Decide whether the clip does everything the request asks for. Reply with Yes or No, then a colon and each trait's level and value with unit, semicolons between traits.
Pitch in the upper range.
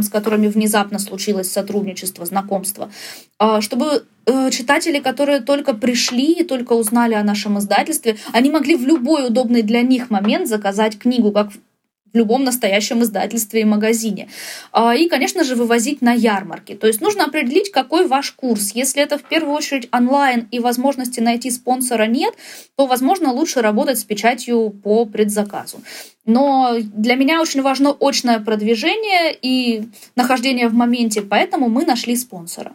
Yes: high, 240 Hz